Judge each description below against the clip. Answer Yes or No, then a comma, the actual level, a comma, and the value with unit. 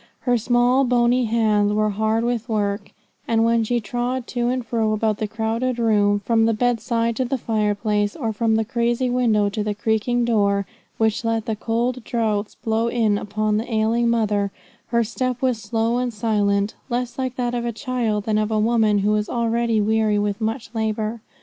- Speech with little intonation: Yes, narrow, 2.0 semitones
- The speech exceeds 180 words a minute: Yes, average, 190 wpm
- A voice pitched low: No, high, 225 Hz